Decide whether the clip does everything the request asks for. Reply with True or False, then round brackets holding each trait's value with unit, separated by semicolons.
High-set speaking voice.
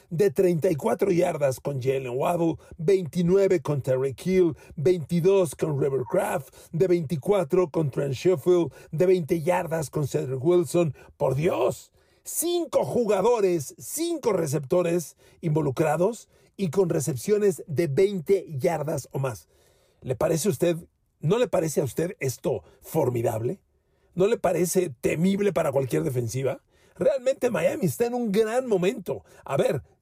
False (175 Hz)